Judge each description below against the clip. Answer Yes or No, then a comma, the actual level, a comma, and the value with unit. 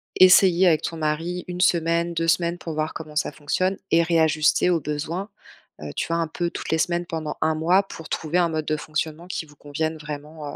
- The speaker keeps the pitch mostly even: Yes, narrow, 2.0 semitones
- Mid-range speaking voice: Yes, medium, 165 Hz